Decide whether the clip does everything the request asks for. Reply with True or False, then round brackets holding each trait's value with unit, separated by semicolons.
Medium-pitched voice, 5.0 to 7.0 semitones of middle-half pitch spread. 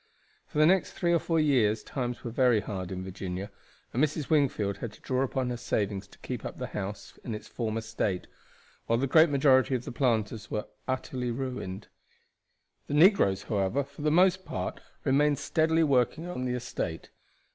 False (125 Hz; 5.5 semitones)